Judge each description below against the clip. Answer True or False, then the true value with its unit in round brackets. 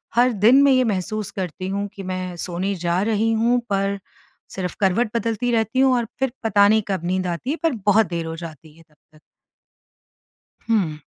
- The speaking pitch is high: True (200 Hz)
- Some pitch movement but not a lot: True (3.9 semitones)